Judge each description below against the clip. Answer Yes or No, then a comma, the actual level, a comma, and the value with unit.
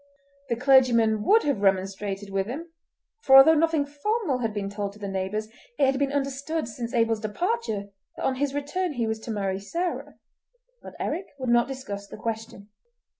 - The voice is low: No, high, 240 Hz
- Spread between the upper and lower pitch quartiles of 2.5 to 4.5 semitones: No, wide, 5.6 semitones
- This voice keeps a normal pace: Yes, average, 180 wpm